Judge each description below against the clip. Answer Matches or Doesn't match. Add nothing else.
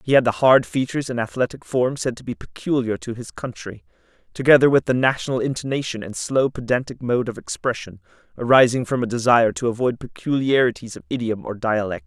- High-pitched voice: Doesn't match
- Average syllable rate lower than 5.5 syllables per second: Doesn't match